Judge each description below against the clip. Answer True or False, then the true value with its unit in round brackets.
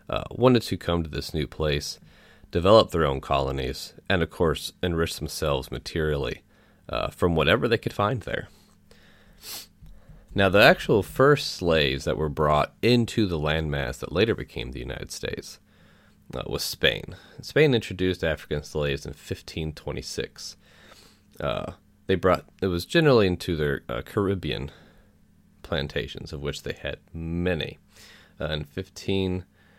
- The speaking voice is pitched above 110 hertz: False (80 Hz)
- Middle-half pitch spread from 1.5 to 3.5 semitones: False (4.4 semitones)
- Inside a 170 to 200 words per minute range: False (145 wpm)